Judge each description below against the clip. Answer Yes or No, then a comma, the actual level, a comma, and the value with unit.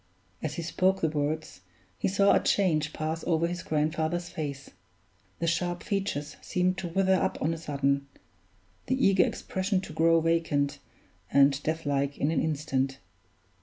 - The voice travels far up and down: No, average, 3.5 semitones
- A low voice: No, medium, 160 Hz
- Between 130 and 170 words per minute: Yes, average, 160 wpm